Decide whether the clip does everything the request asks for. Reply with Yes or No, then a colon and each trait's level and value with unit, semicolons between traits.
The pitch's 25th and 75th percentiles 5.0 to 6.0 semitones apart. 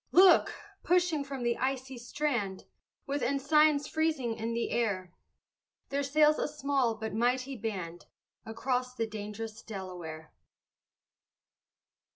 No: average, 4.4 semitones